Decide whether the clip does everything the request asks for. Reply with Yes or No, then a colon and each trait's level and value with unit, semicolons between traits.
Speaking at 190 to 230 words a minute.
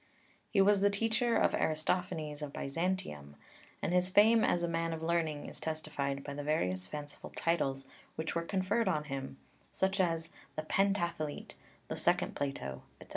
No: average, 165 wpm